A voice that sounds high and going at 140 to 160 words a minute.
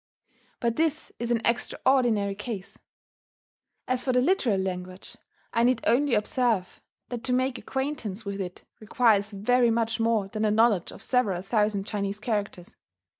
Yes: high, 225 Hz; average, 150 wpm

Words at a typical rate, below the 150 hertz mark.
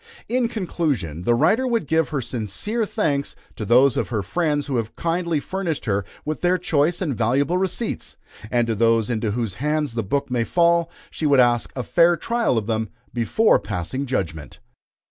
Yes: average, 185 wpm; medium, 140 Hz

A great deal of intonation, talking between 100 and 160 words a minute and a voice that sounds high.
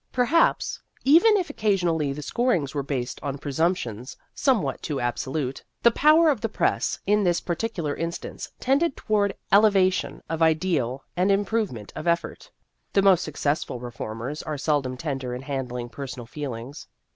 No: wide, 7.3 semitones; average, 155 wpm; medium, 160 Hz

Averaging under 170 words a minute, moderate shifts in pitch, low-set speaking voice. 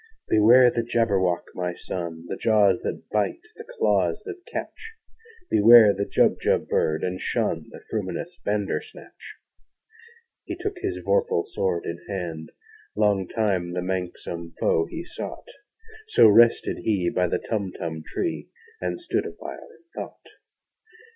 No: slow, 135 wpm; wide, 6.3 semitones; low, 105 Hz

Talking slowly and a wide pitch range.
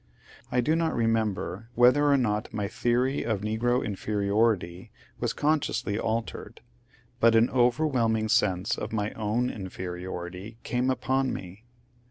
No: slow, 130 wpm; average, 3.2 semitones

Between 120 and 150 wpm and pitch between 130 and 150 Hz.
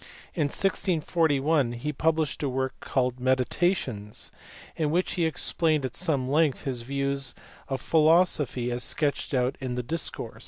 Yes: average, 145 wpm; medium, 140 Hz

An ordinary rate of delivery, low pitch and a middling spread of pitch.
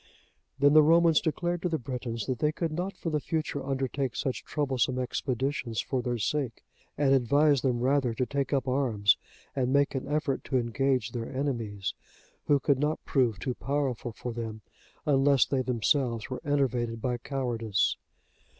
Yes: average, 170 wpm; low, 130 Hz; average, 3.1 semitones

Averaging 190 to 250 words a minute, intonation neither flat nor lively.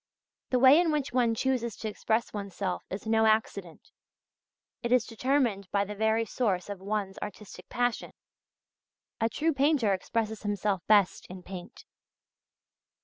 No: average, 145 wpm; average, 3.5 semitones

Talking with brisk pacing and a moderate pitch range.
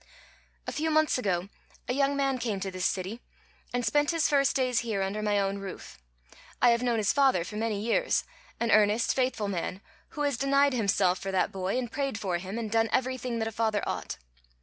Yes: fast, 210 wpm; average, 4.6 semitones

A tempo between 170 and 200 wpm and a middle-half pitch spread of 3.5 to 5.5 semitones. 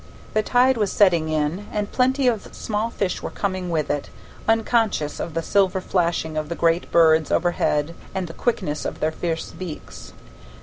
Yes: average, 175 wpm; average, 4.8 semitones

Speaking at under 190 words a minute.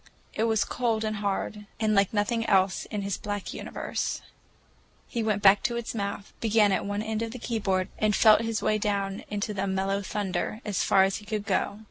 No: fast, 205 wpm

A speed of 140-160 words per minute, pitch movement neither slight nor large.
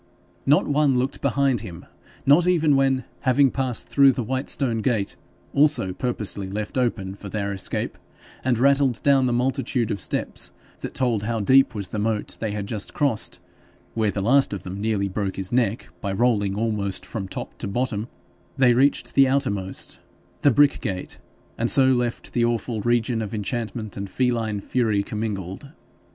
No: average, 170 wpm; average, 4.4 semitones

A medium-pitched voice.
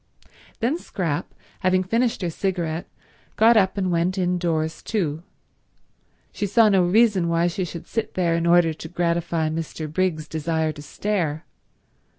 Yes: medium, 175 Hz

